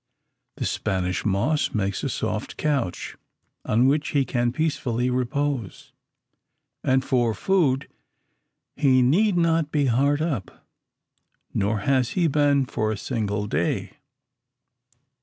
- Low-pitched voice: Yes, low, 130 Hz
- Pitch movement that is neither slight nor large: Yes, average, 4.9 semitones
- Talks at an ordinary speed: No, slow, 120 wpm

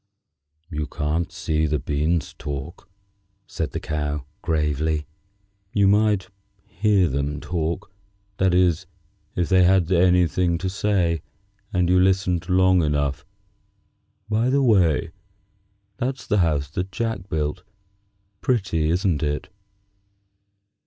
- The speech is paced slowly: Yes, slow, 115 wpm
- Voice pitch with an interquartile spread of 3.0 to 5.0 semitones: Yes, average, 3.8 semitones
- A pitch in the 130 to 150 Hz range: No, very low, 85 Hz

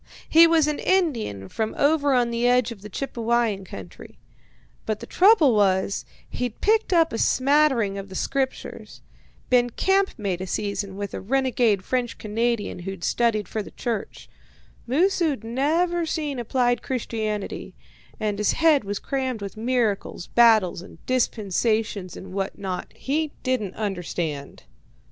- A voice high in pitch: Yes, high, 235 Hz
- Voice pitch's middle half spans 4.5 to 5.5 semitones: Yes, average, 5.2 semitones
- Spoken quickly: No, average, 145 wpm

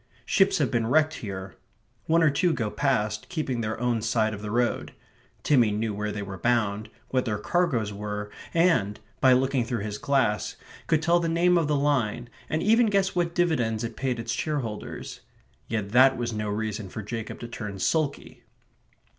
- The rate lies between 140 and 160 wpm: No, average, 185 wpm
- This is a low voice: Yes, low, 120 Hz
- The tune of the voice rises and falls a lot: Yes, wide, 5.9 semitones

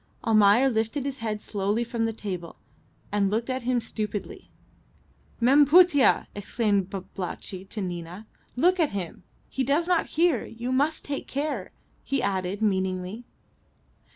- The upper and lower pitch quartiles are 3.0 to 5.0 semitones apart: No, wide, 5.6 semitones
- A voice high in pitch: Yes, high, 225 Hz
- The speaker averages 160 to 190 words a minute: No, average, 140 wpm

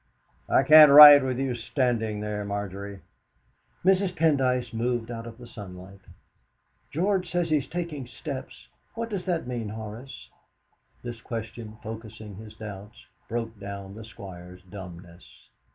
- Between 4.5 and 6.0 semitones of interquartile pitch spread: Yes, average, 5.0 semitones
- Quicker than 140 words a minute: No, slow, 135 wpm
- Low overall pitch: Yes, low, 115 Hz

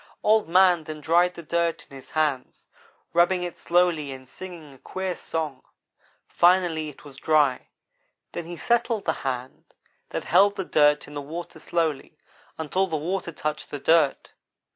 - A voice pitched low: No, medium, 165 Hz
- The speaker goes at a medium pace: Yes, average, 165 wpm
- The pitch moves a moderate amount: Yes, average, 3.2 semitones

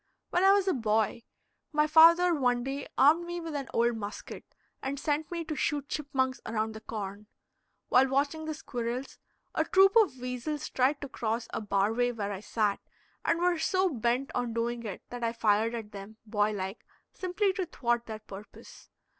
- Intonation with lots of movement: Yes, wide, 5.8 semitones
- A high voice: Yes, very high, 250 Hz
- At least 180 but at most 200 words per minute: Yes, average, 190 wpm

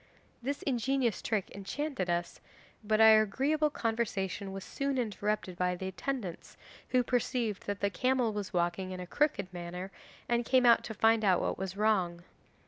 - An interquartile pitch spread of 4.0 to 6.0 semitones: Yes, average, 4.6 semitones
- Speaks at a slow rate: No, average, 160 wpm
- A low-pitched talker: No, high, 215 Hz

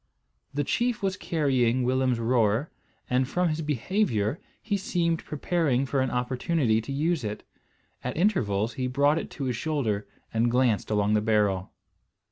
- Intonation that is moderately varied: No, wide, 5.8 semitones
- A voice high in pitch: No, low, 130 Hz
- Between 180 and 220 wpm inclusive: No, average, 155 wpm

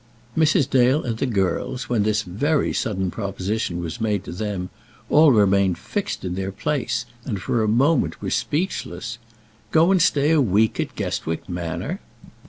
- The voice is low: Yes, low, 110 Hz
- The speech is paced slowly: No, average, 165 wpm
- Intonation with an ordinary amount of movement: No, wide, 6.2 semitones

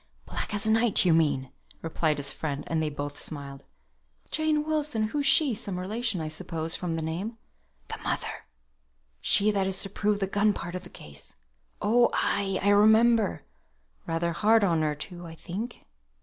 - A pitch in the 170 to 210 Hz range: Yes, high, 190 Hz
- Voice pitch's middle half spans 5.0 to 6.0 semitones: Yes, average, 5.3 semitones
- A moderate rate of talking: Yes, average, 175 wpm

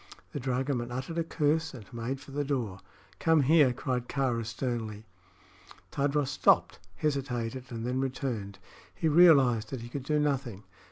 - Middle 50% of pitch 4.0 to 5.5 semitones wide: No, average, 3.4 semitones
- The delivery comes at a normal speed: Yes, average, 155 wpm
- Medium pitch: No, low, 130 Hz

